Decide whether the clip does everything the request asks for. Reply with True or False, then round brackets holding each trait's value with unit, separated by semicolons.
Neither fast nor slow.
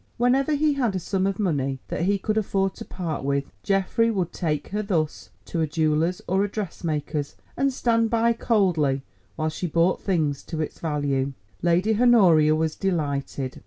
True (175 wpm)